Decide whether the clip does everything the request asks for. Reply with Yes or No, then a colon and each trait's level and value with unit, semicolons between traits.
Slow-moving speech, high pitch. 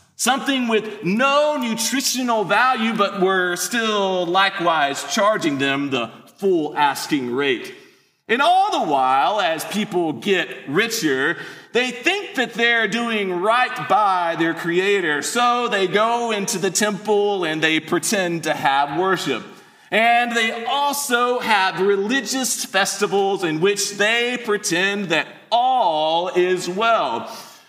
Yes: slow, 125 wpm; high, 210 Hz